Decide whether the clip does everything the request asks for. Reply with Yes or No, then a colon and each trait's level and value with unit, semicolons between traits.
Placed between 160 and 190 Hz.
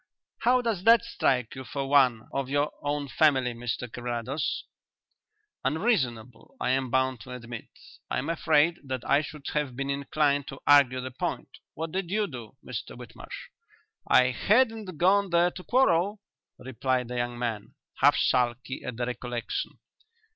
No: low, 135 Hz